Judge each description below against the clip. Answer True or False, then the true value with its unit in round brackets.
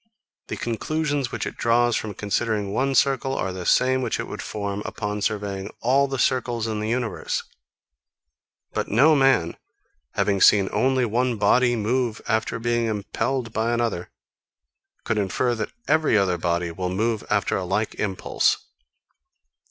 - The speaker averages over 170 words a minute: False (150 wpm)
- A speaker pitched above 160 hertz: False (115 Hz)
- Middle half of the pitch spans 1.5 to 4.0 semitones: True (3.7 semitones)